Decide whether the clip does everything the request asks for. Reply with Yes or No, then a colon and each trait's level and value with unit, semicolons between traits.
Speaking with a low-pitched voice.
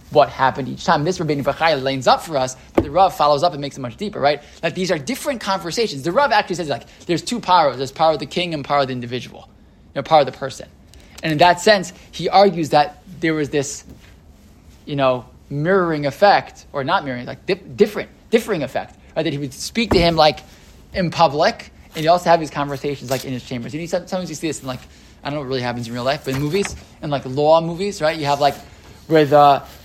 No: medium, 150 Hz